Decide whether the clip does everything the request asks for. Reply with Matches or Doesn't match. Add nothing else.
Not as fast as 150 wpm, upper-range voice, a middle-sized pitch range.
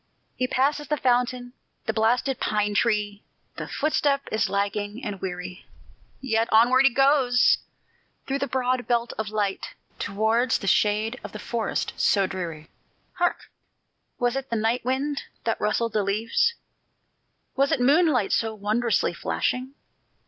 Matches